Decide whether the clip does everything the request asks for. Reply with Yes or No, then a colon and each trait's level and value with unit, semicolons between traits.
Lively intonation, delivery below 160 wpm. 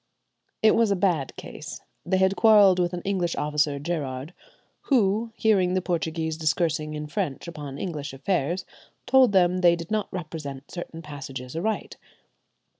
No: average, 4.1 semitones; average, 150 wpm